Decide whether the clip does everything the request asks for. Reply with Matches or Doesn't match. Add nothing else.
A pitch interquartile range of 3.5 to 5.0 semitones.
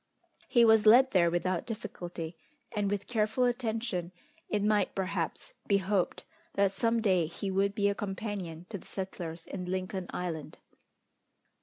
Doesn't match